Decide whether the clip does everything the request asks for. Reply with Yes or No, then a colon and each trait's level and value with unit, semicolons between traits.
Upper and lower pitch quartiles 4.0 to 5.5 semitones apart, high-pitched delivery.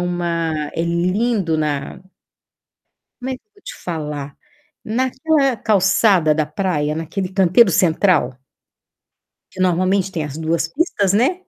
No: average, 4.5 semitones; medium, 180 Hz